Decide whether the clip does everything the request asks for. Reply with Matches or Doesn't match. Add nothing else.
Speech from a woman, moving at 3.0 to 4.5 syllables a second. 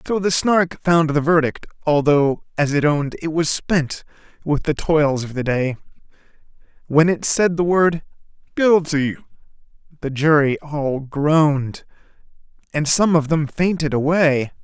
Doesn't match